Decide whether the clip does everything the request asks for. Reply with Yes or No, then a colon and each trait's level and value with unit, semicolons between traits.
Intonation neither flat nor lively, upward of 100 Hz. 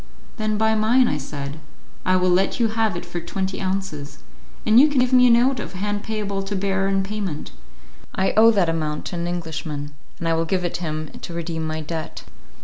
Yes: average, 4.7 semitones; high, 190 Hz